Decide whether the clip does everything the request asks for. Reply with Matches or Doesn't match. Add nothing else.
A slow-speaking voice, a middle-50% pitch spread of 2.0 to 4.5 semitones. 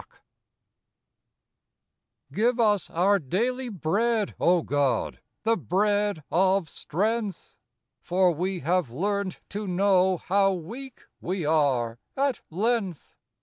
Matches